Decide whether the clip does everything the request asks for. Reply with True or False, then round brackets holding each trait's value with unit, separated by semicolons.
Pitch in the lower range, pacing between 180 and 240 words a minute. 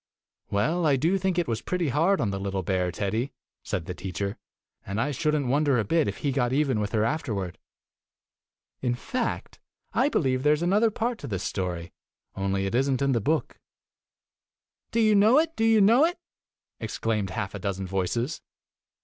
True (130 Hz; 190 wpm)